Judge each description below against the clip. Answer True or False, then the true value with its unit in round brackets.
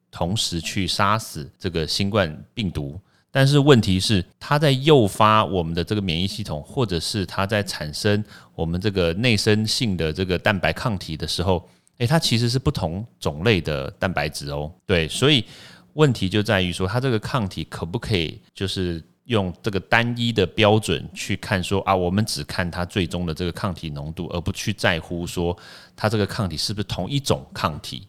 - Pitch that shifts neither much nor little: True (4.3 semitones)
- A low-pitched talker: True (100 Hz)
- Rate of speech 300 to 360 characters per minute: False (280 characters per minute)